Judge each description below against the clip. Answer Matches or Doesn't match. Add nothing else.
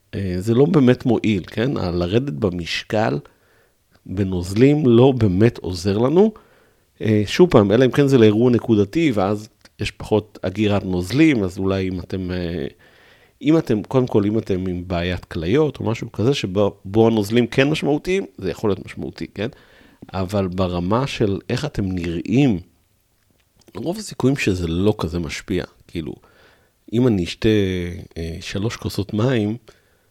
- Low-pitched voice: Matches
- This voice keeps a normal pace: Matches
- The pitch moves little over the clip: Doesn't match